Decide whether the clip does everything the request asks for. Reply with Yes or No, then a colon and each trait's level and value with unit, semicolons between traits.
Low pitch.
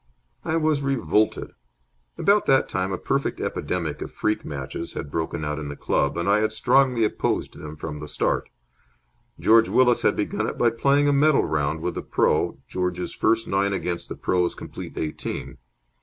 Yes: very low, 95 Hz